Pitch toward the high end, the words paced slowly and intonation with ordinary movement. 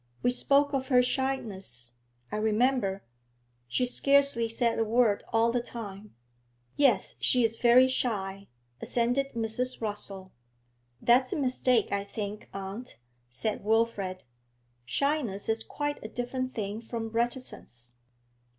Yes: high, 230 Hz; slow, 125 wpm; average, 3.6 semitones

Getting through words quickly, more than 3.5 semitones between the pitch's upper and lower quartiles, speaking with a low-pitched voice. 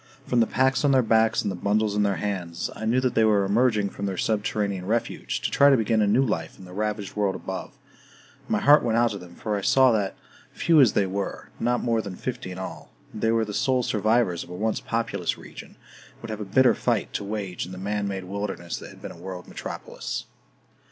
No: fast, 240 wpm; average, 3.0 semitones; low, 105 Hz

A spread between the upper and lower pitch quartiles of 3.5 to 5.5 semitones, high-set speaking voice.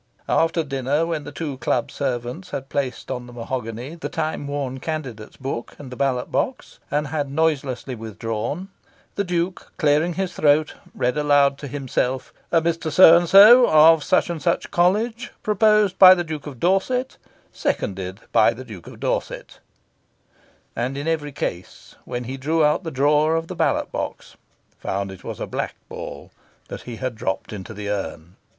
No: average, 4.9 semitones; medium, 145 Hz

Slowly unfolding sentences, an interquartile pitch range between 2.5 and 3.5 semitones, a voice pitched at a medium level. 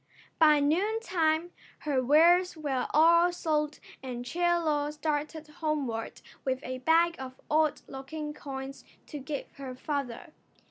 No: slow, 130 wpm; average, 3.2 semitones; very high, 300 Hz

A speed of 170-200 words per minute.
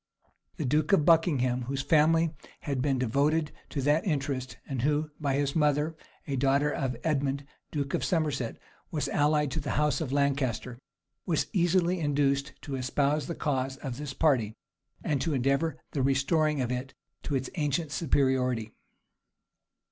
No: average, 155 wpm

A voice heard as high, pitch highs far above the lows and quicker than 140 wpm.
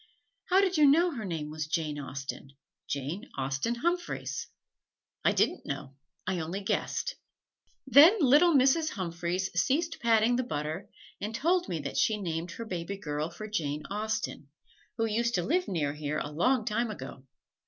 Yes: high, 205 Hz; wide, 9.0 semitones; average, 165 wpm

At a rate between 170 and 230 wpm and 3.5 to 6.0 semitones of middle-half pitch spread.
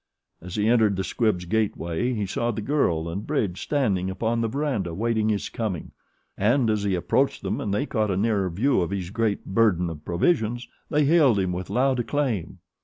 Yes: average, 195 wpm; average, 4.4 semitones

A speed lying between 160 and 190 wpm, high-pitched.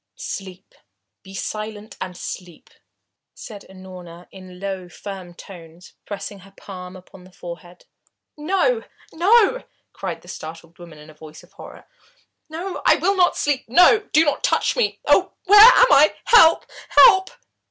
No: average, 150 wpm; high, 195 Hz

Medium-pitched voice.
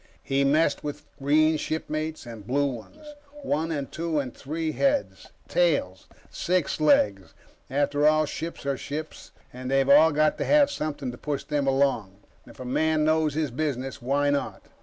Yes: medium, 145 Hz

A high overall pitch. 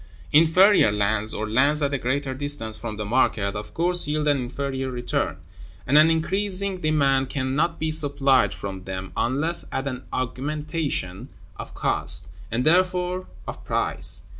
No: medium, 140 Hz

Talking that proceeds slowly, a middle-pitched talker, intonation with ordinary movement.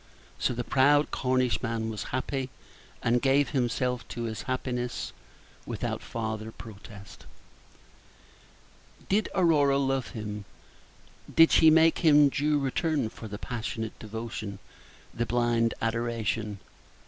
No: slow, 115 wpm; low, 120 Hz; average, 3.6 semitones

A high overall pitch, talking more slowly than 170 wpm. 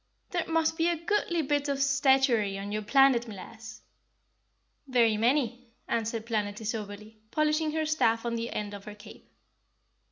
Yes: high, 235 Hz; average, 155 wpm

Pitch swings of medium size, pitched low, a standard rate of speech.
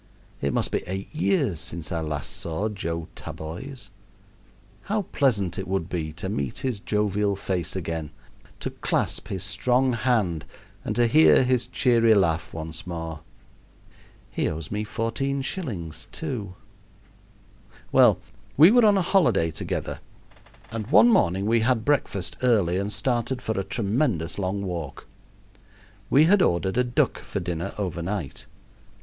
No: wide, 6.7 semitones; low, 100 Hz; average, 145 wpm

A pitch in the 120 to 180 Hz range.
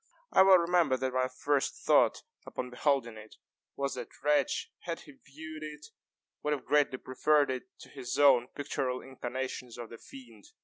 Yes: low, 135 Hz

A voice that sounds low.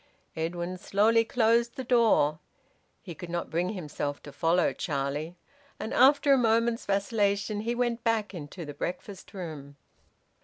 No: high, 195 Hz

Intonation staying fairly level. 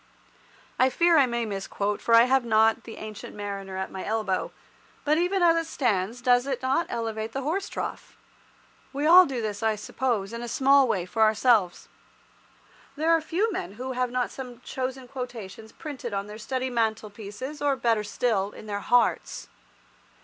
No: average, 3.9 semitones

